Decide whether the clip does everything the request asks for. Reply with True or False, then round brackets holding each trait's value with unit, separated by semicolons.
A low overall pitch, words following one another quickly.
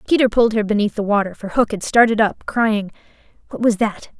False (215 Hz; 215 wpm)